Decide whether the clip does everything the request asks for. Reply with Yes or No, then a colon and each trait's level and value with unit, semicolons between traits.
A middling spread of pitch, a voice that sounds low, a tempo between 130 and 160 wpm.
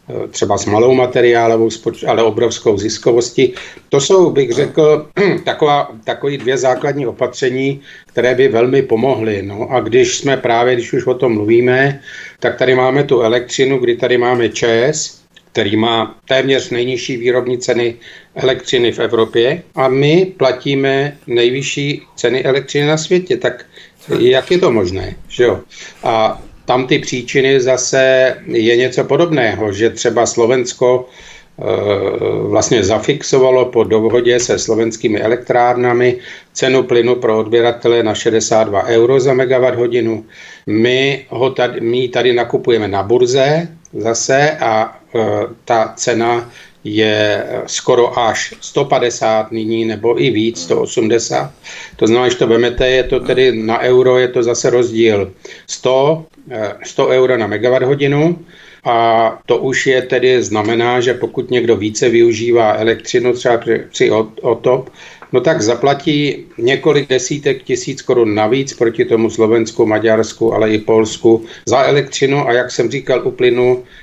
Yes: average, 3.0 semitones; low, 125 Hz; average, 140 wpm